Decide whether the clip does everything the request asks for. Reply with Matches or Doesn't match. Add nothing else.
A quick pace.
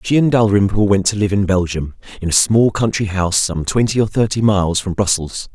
Matches